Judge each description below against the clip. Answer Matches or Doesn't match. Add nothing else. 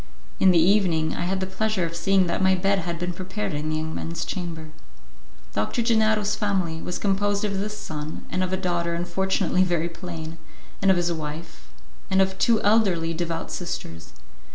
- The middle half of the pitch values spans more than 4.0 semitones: Doesn't match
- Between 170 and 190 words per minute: Matches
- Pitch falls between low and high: Matches